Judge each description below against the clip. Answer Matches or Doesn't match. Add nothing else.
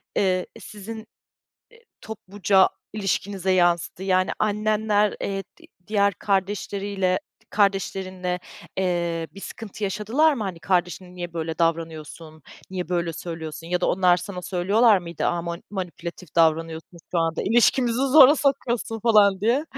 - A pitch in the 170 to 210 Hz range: Matches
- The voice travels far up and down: Doesn't match